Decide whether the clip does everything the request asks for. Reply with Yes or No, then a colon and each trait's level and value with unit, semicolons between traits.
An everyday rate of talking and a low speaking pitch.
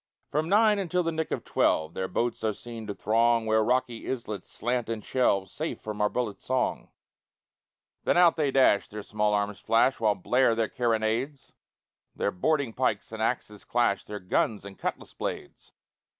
Yes: average, 175 wpm; low, 115 Hz